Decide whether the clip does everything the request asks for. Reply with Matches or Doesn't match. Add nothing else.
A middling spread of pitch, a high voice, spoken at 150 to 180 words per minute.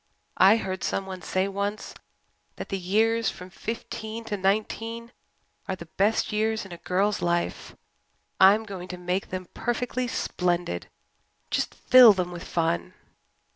Doesn't match